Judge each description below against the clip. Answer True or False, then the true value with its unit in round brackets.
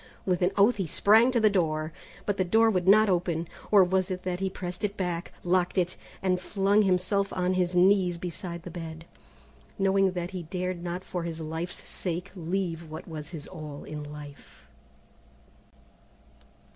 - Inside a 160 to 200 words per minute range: True (175 wpm)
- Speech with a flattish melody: True (2.3 semitones)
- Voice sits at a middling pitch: True (180 Hz)